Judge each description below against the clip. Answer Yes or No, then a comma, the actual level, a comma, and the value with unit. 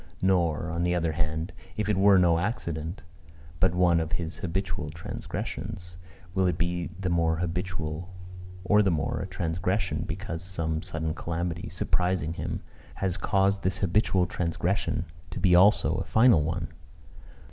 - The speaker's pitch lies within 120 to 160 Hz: No, very low, 90 Hz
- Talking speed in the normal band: Yes, average, 150 wpm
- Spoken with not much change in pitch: Yes, narrow, 2.3 semitones